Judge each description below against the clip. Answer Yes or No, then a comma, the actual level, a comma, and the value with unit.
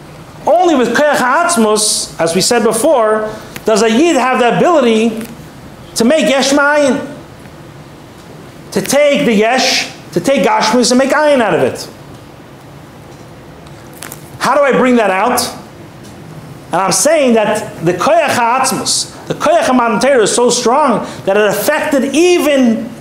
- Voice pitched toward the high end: Yes, high, 245 Hz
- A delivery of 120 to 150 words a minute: Yes, average, 140 wpm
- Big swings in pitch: No, average, 4.6 semitones